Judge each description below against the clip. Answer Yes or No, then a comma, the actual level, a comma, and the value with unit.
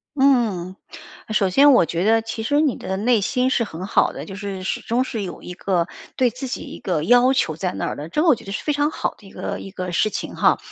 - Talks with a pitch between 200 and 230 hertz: Yes, high, 215 Hz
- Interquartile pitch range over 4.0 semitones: Yes, average, 5.3 semitones